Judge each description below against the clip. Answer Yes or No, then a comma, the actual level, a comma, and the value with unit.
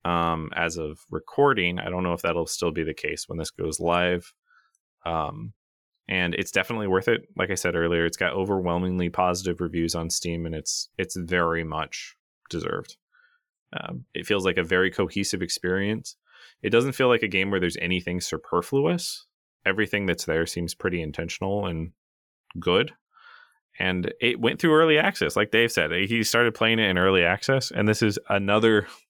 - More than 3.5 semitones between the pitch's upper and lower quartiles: Yes, average, 4.0 semitones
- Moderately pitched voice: No, very low, 90 Hz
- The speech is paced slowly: No, average, 175 wpm